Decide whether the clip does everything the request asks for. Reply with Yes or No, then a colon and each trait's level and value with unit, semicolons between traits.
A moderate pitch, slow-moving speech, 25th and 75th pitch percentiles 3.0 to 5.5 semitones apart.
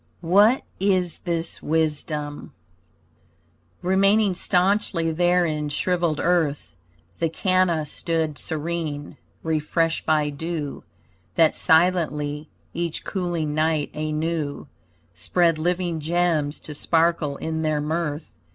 No: medium, 160 Hz; slow, 100 wpm; narrow, 2.4 semitones